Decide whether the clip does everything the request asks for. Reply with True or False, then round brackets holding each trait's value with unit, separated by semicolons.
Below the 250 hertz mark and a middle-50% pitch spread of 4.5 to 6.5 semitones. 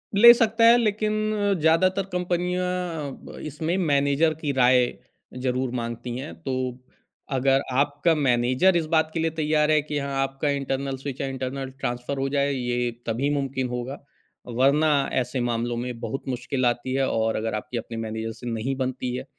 False (135 Hz; 4.0 semitones)